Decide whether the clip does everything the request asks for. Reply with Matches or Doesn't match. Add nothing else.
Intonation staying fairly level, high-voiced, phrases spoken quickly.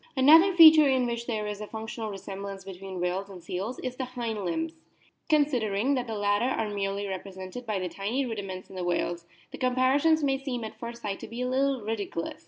Doesn't match